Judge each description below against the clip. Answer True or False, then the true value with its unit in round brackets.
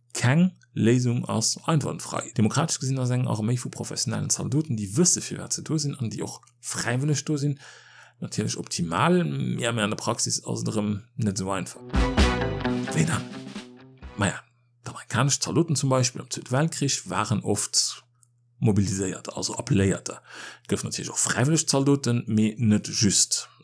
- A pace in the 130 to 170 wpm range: True (145 wpm)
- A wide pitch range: False (4.7 semitones)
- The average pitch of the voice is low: True (125 Hz)